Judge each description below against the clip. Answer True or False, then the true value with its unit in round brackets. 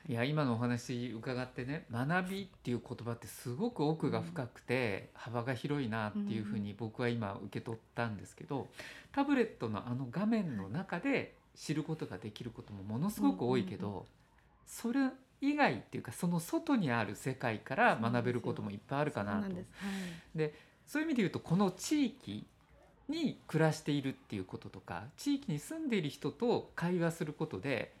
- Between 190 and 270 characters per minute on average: False (300 characters per minute)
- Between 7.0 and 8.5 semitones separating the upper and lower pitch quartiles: True (7.6 semitones)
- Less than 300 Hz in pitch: True (135 Hz)